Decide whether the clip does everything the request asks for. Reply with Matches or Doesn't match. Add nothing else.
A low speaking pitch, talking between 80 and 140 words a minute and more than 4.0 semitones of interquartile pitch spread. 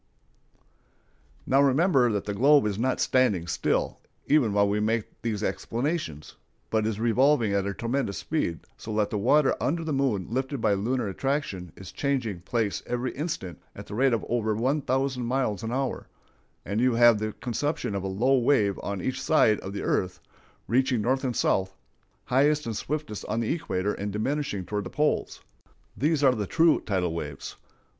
Doesn't match